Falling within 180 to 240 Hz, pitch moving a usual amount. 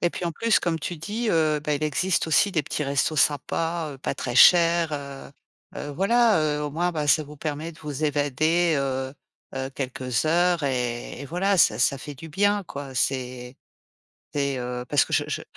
No: medium, 150 Hz; average, 3.7 semitones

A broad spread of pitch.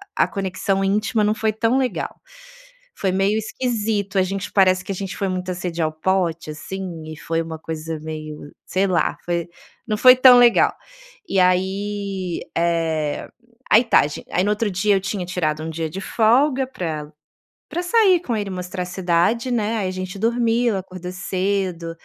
No: average, 3.8 semitones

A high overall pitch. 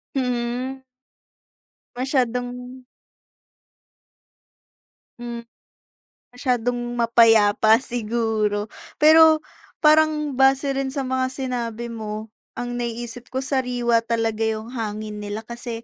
Yes: high, 240 Hz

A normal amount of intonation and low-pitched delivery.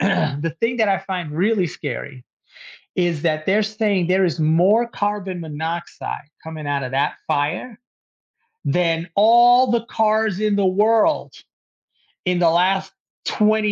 No: average, 4.8 semitones; medium, 185 Hz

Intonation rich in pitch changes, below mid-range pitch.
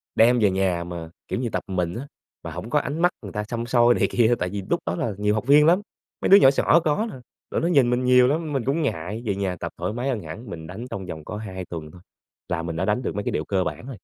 Yes: wide, 5.7 semitones; low, 110 Hz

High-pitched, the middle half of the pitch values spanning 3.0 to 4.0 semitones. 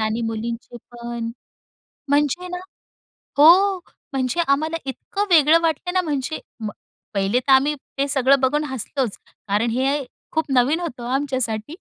No: very high, 275 Hz; average, 4.7 semitones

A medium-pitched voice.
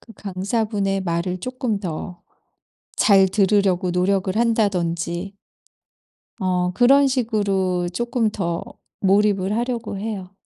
No: high, 195 Hz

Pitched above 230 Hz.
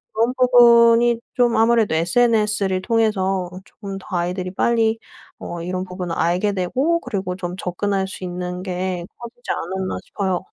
No: high, 195 Hz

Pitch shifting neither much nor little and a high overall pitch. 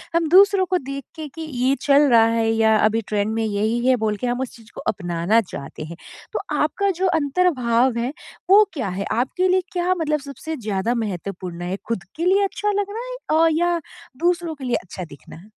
No: wide, 7.8 semitones; very high, 250 Hz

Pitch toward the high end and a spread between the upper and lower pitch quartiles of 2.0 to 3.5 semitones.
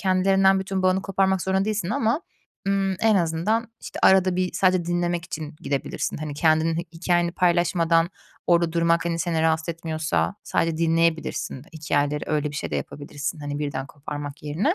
No: medium, 170 Hz; average, 3.1 semitones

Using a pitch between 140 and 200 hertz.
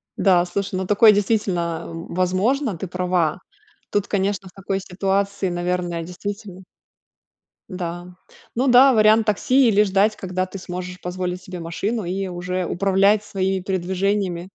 Yes: high, 190 Hz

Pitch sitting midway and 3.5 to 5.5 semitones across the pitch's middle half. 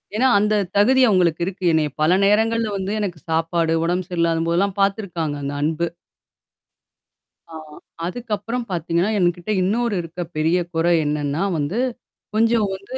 Yes: medium, 180 Hz; average, 4.2 semitones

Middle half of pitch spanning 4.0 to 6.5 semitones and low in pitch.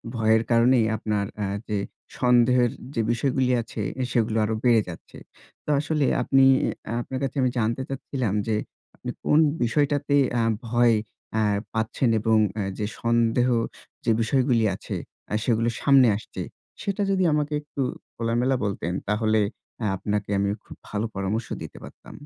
No: average, 3.0 semitones; low, 115 Hz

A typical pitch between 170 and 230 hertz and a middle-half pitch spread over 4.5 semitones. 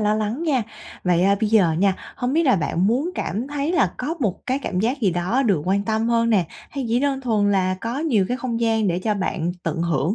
Yes: high, 220 Hz; average, 5.2 semitones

